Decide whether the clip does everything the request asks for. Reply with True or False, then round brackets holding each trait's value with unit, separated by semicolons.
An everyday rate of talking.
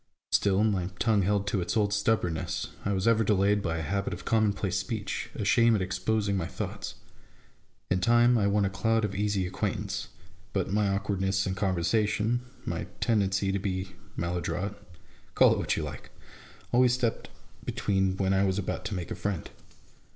True (180 wpm)